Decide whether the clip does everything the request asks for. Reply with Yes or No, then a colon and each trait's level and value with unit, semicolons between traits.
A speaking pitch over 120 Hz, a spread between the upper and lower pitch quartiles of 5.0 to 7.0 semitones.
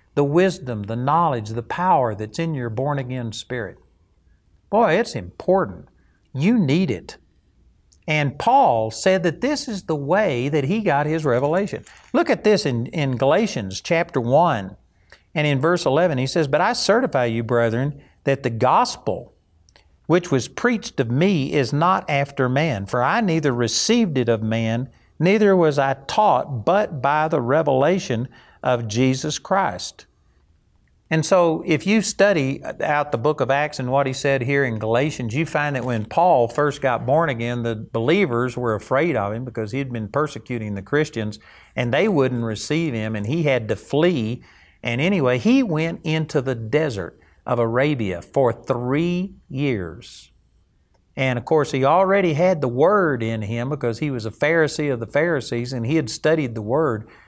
Yes: low, 135 Hz; wide, 5.5 semitones